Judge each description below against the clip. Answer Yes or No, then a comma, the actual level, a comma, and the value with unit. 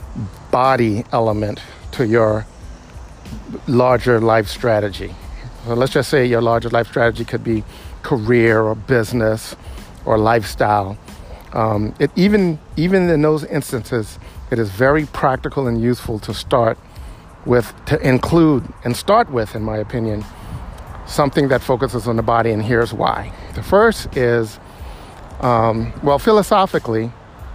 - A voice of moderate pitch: No, low, 115 Hz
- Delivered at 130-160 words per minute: Yes, slow, 135 wpm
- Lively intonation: No, average, 3.3 semitones